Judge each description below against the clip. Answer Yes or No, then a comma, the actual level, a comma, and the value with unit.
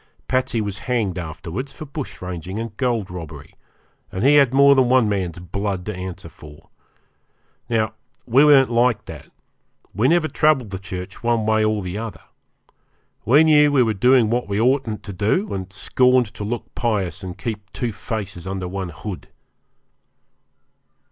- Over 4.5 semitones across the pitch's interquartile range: Yes, average, 5.1 semitones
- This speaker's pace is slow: No, average, 165 wpm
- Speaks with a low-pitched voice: Yes, low, 110 Hz